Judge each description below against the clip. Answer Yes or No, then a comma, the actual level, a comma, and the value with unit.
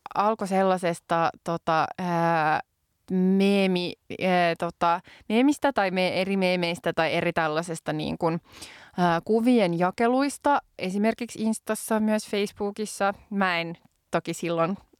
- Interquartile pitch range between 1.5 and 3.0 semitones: No, average, 3.7 semitones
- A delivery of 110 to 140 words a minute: No, slow, 95 wpm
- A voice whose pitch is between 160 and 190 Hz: Yes, medium, 185 Hz